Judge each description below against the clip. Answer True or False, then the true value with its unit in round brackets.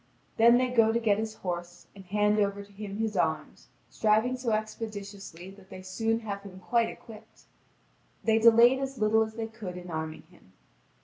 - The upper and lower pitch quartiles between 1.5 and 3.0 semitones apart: True (2.4 semitones)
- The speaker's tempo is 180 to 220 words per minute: True (185 wpm)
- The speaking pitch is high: True (215 Hz)